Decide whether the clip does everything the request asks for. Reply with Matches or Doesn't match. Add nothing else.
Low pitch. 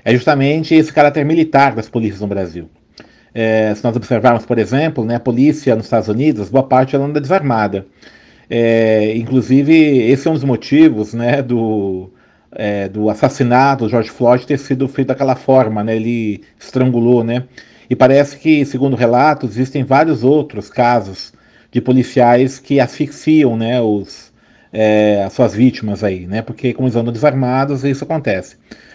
Matches